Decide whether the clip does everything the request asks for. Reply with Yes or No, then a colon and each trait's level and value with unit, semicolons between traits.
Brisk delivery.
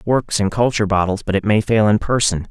Yes: fast, 265 wpm